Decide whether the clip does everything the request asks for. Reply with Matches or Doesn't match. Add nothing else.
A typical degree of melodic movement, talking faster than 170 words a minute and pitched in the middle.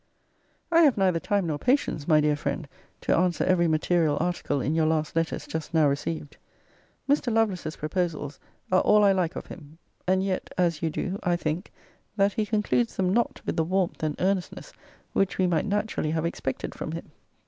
Matches